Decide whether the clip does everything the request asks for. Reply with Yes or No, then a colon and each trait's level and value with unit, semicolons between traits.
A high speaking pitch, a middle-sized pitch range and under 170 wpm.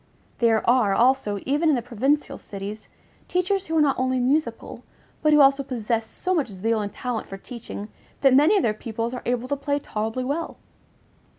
No: very high, 255 Hz; average, 4.4 semitones; average, 190 wpm